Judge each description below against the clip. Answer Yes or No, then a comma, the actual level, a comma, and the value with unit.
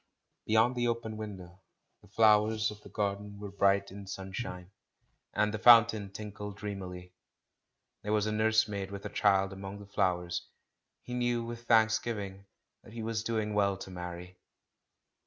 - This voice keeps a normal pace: Yes, average, 160 wpm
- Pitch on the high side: No, low, 105 Hz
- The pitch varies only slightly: Yes, narrow, 2.2 semitones